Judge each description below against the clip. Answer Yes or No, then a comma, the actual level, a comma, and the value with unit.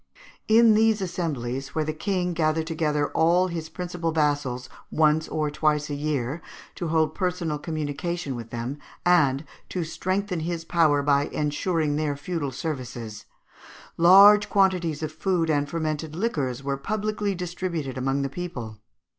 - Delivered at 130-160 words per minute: Yes, average, 150 wpm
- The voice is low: No, medium, 155 Hz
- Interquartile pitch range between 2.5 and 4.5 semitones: Yes, average, 3.7 semitones